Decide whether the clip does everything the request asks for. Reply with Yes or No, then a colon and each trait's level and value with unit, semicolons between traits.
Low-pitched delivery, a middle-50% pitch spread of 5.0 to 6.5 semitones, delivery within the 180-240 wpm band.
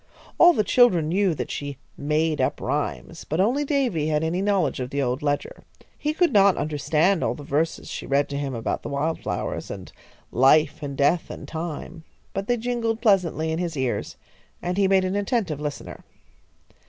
No: medium, 165 Hz; wide, 5.4 semitones; average, 190 wpm